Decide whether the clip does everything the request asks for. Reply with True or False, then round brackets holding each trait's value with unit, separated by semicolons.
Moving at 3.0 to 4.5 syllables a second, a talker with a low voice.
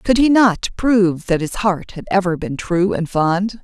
False (4.3 syllables/s; 190 Hz)